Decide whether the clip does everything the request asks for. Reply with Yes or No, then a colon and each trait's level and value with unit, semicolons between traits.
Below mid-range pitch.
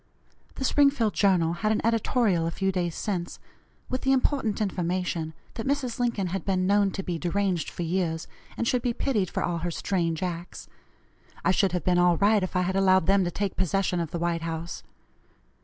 No: medium, 185 Hz